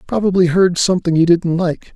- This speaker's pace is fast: No, average, 185 wpm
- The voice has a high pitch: No, medium, 175 Hz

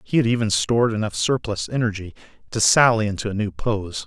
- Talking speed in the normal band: Yes, average, 190 wpm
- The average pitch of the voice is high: No, low, 110 Hz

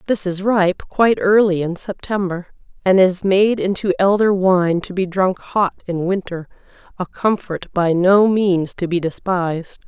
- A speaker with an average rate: Yes, average, 165 wpm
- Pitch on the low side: No, medium, 185 Hz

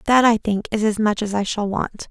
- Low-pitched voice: No, high, 215 Hz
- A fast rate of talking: Yes, fast, 285 wpm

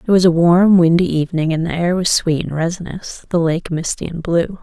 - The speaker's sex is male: No, female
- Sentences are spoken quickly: Yes, fast, 235 wpm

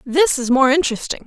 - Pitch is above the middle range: Yes, very high, 280 Hz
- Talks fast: No, average, 190 wpm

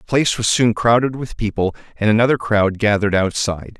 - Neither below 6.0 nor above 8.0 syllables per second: Yes, 6.2 syllables/s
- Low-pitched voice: Yes, low, 110 Hz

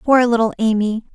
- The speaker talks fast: No, average, 155 wpm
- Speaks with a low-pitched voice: No, high, 225 Hz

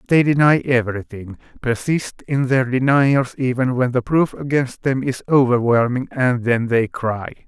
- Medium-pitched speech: No, low, 125 Hz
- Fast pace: No, average, 155 wpm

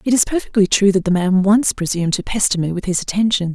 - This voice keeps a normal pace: No, fast, 255 wpm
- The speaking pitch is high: Yes, high, 195 Hz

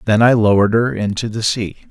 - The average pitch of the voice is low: Yes, low, 110 Hz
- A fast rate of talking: Yes, fast, 220 wpm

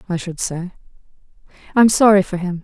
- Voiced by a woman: Yes, female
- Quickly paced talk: No, average, 185 wpm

